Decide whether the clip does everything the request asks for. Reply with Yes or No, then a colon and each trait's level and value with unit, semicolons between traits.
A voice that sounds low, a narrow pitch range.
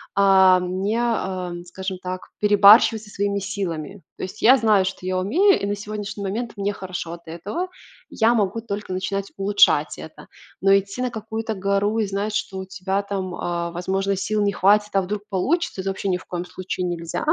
No: high, 195 Hz; narrow, 2.0 semitones